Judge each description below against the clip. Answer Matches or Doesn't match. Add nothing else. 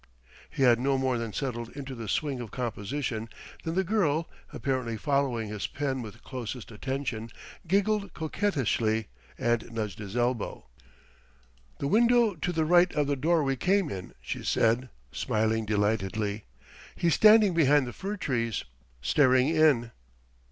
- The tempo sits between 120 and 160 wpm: Matches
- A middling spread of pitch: Doesn't match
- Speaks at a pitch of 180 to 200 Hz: Doesn't match